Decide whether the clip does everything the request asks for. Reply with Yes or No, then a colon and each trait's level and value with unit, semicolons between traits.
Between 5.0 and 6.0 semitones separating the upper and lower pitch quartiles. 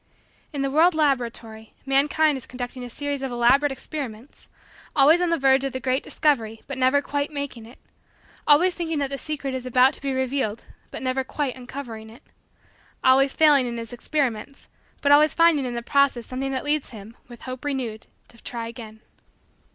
No: average, 3.0 semitones